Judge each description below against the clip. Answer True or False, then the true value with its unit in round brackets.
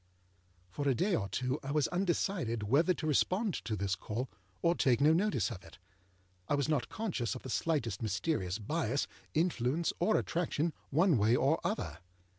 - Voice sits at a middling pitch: True (145 Hz)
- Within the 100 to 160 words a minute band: False (175 wpm)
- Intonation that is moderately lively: False (6.8 semitones)